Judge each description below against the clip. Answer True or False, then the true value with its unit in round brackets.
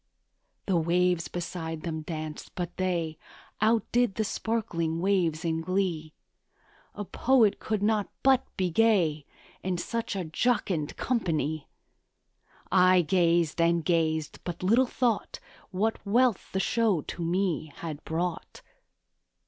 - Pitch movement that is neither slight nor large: True (4.2 semitones)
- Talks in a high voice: False (180 Hz)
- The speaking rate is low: True (125 wpm)